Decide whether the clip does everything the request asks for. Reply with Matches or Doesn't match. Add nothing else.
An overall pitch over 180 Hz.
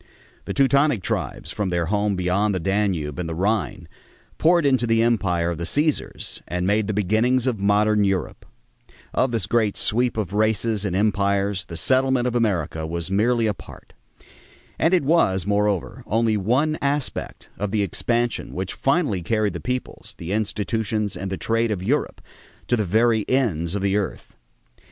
Doesn't match